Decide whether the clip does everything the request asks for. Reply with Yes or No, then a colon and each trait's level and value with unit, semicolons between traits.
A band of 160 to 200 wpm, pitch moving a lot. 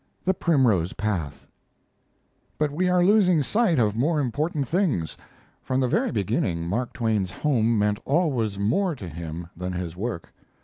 No: average, 150 wpm; wide, 8.6 semitones